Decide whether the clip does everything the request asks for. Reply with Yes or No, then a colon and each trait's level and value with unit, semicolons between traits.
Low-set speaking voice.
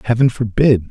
Yes: low, 115 Hz